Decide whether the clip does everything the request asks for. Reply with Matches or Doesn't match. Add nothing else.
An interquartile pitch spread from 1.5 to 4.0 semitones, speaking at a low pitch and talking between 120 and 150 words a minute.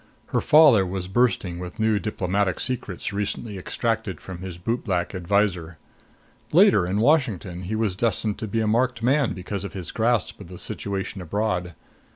Doesn't match